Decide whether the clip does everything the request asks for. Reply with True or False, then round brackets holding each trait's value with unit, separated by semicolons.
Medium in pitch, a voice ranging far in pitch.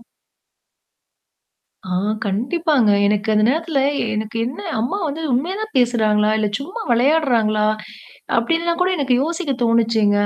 False (245 Hz; 7.0 semitones)